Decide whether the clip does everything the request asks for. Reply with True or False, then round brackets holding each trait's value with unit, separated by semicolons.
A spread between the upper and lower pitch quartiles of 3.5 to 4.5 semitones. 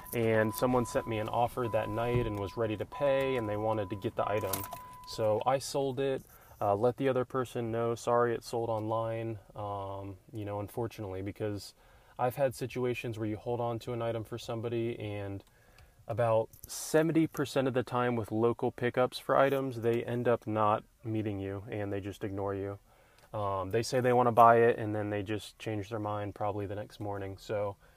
False (2.6 semitones)